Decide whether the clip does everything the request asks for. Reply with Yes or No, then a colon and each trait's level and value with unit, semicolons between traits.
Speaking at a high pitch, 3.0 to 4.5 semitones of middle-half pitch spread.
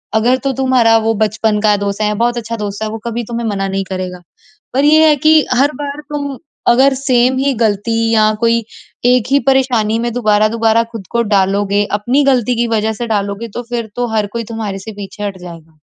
Yes: high, 225 Hz; average, 3.3 semitones